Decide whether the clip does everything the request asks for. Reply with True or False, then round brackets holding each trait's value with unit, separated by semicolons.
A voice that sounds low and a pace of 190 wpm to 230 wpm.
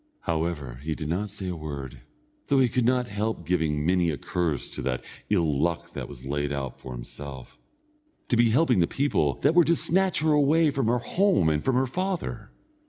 True (90 Hz; 205 wpm)